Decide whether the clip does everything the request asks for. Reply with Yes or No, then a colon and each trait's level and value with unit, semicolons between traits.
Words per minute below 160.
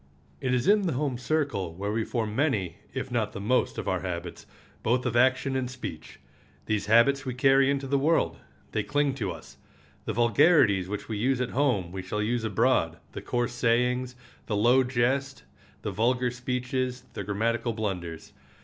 No: average, 175 wpm